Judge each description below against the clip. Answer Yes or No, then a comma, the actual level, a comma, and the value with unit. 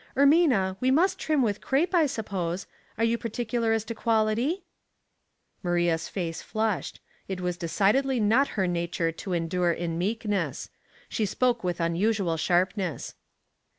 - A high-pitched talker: Yes, high, 205 Hz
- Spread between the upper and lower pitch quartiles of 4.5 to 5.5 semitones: Yes, average, 5.2 semitones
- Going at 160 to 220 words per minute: No, average, 145 wpm